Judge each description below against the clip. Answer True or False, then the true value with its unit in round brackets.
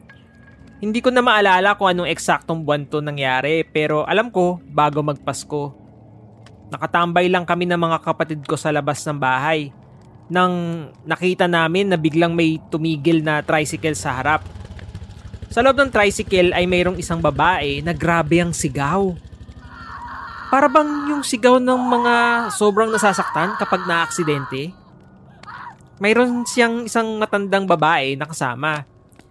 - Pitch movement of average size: True (4.9 semitones)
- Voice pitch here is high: False (165 Hz)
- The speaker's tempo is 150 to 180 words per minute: False (135 wpm)